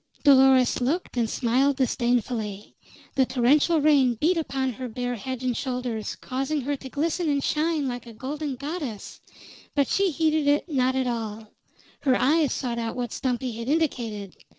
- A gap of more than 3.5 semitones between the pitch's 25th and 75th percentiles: No, average, 3.2 semitones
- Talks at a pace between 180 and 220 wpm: No, average, 165 wpm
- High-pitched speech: Yes, very high, 260 Hz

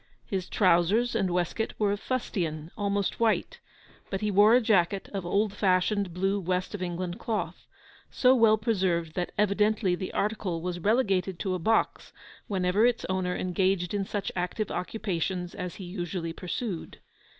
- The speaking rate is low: No, average, 160 wpm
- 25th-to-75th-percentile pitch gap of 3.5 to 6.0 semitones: No, average, 2.9 semitones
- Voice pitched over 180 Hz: Yes, high, 190 Hz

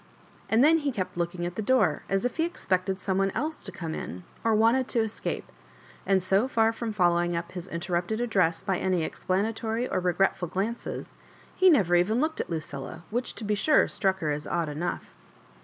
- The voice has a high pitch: Yes, high, 195 Hz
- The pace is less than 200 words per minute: No, fast, 205 wpm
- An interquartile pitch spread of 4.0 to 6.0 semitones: Yes, average, 4.6 semitones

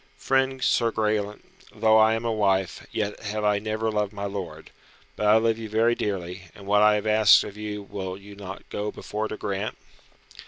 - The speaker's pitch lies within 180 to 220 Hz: No, low, 105 Hz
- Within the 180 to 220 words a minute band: Yes, average, 200 wpm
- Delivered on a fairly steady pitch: Yes, narrow, 1.5 semitones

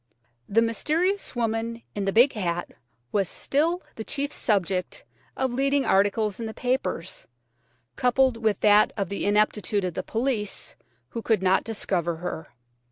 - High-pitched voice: Yes, high, 220 Hz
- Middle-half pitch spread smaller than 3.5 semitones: No, average, 4.2 semitones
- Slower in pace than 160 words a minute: Yes, average, 150 wpm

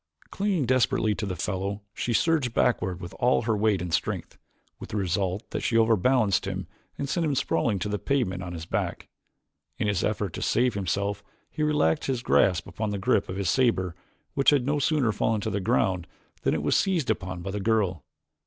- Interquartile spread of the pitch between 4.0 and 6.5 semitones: Yes, average, 5.2 semitones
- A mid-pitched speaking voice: No, low, 105 Hz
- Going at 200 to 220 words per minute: Yes, fast, 205 wpm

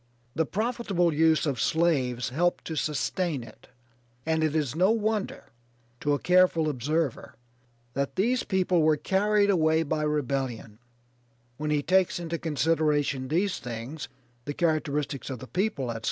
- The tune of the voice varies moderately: Yes, average, 4.1 semitones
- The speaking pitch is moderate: Yes, medium, 155 Hz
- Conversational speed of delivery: Yes, average, 145 wpm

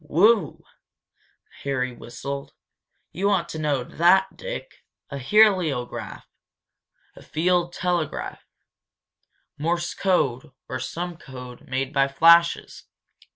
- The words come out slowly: Yes, slow, 95 wpm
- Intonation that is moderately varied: Yes, average, 4.8 semitones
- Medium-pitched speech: Yes, medium, 160 Hz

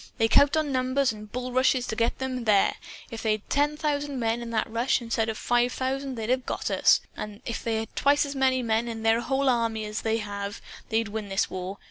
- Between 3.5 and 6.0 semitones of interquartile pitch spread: No, average, 2.9 semitones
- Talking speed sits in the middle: No, fast, 230 wpm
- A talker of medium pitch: No, high, 235 Hz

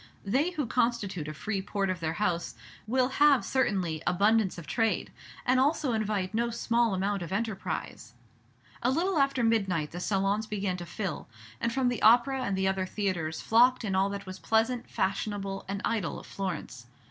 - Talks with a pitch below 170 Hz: No, high, 205 Hz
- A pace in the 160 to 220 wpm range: Yes, average, 180 wpm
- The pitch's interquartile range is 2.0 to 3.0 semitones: No, average, 4.0 semitones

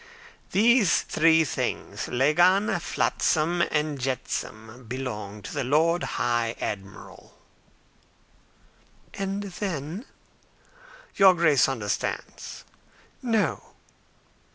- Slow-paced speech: Yes, slow, 80 wpm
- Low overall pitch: No, medium, 155 Hz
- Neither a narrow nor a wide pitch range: No, wide, 6.5 semitones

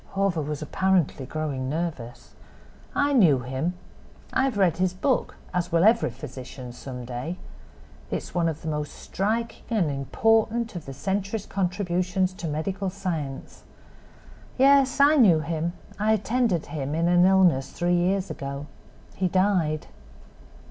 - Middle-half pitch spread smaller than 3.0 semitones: No, average, 4.8 semitones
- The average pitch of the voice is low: No, medium, 175 Hz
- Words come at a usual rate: Yes, average, 145 wpm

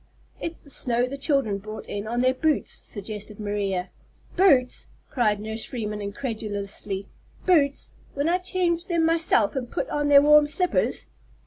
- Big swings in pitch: Yes, wide, 6.2 semitones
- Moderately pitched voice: No, very high, 250 Hz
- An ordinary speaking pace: Yes, average, 150 wpm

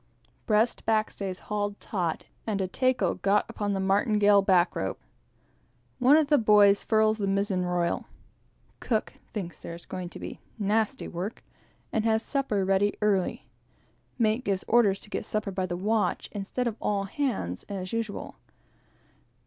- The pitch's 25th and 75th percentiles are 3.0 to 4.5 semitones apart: No, narrow, 2.4 semitones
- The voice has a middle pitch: No, high, 205 Hz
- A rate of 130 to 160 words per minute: Yes, average, 150 wpm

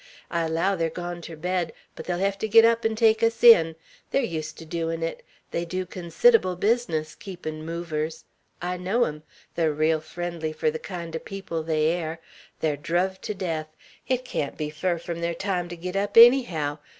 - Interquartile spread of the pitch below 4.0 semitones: Yes, average, 3.4 semitones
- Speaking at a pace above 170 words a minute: Yes, average, 195 wpm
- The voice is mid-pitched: Yes, medium, 170 Hz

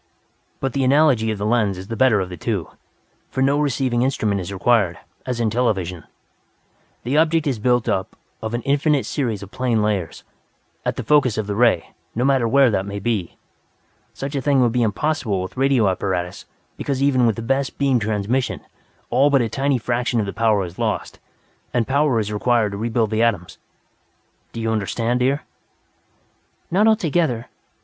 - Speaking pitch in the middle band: No, low, 120 Hz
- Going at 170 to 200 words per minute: Yes, average, 185 wpm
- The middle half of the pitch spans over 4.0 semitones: Yes, average, 4.4 semitones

